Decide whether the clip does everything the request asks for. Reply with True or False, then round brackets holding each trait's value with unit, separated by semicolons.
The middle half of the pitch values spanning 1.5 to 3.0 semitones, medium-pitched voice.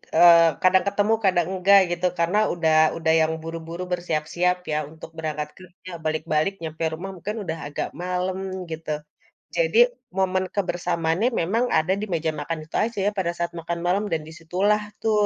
True (2.7 semitones; 175 Hz)